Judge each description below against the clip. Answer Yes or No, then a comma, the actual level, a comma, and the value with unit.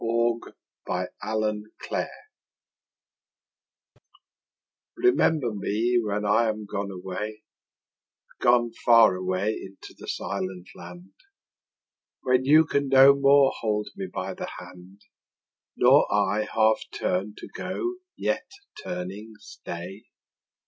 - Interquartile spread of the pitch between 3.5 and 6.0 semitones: Yes, average, 4.1 semitones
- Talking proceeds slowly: Yes, slow, 105 wpm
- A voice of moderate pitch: No, low, 110 Hz